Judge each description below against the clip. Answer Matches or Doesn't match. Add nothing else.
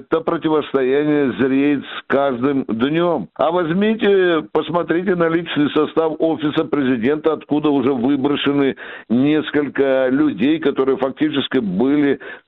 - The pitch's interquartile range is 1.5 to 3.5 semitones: Matches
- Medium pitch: Matches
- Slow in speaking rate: Matches